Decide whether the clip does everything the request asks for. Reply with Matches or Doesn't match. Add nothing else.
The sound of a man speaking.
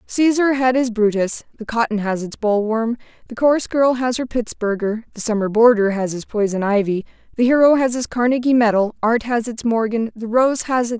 Doesn't match